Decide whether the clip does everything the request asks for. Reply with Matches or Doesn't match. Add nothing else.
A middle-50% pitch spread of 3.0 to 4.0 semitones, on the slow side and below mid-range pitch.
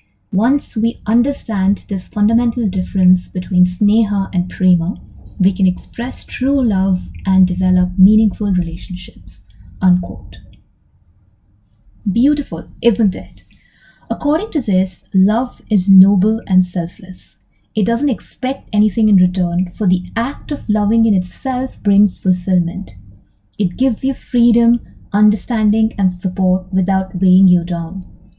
Doesn't match